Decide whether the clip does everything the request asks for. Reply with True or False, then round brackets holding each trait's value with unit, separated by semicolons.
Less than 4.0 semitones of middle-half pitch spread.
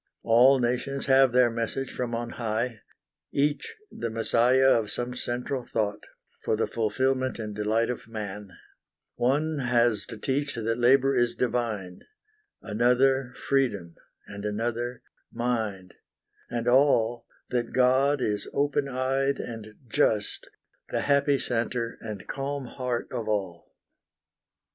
True (3.0 semitones)